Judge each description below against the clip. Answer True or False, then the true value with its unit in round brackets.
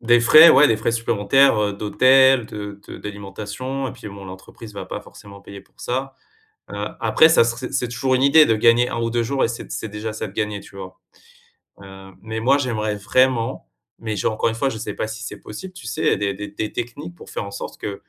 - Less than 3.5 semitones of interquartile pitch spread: False (3.9 semitones)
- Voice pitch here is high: False (115 Hz)